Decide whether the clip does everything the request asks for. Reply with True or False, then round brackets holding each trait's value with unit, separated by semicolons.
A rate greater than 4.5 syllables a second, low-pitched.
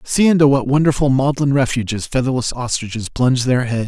True (5.8 syllables/s; 130 Hz)